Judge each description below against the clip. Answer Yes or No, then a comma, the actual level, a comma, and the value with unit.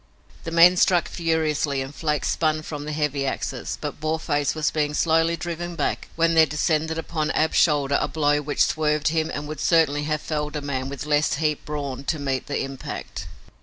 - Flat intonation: Yes, narrow, 1.7 semitones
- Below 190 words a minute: No, average, 195 wpm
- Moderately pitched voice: Yes, medium, 150 Hz